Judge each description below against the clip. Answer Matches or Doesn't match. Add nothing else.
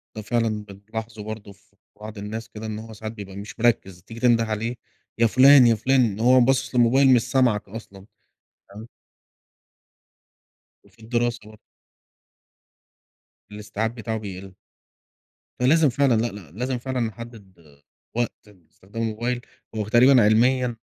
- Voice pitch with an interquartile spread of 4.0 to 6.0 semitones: Doesn't match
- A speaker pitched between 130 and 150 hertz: Doesn't match